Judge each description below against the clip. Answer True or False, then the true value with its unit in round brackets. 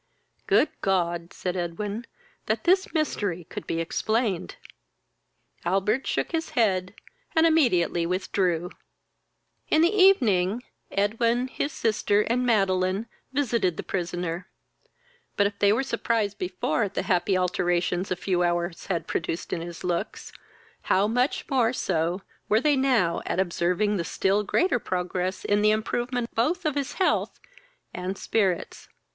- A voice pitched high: True (200 Hz)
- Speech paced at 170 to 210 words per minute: False (140 wpm)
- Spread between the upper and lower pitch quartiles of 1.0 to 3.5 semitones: False (4.9 semitones)